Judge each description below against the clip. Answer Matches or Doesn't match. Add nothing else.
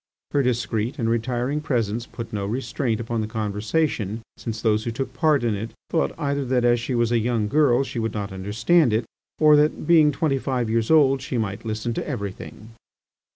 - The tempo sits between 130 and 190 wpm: Doesn't match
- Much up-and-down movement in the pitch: Doesn't match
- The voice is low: Matches